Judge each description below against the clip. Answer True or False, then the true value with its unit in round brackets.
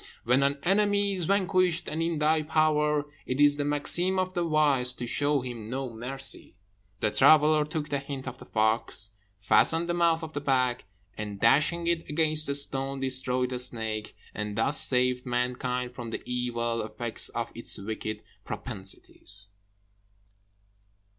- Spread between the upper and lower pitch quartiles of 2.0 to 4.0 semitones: False (4.4 semitones)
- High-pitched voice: False (135 Hz)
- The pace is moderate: True (160 wpm)